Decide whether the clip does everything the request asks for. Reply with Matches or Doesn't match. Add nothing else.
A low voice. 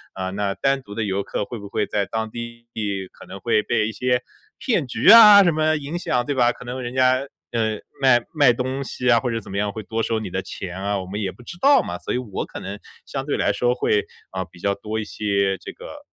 Matches